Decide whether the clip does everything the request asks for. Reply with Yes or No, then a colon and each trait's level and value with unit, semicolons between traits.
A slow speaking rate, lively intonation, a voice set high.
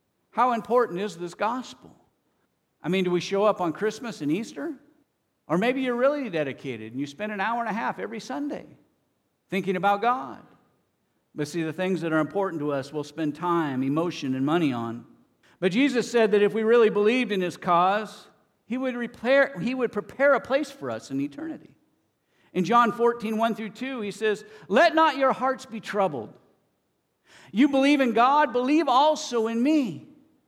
No: average, 185 wpm; wide, 6.0 semitones; high, 215 Hz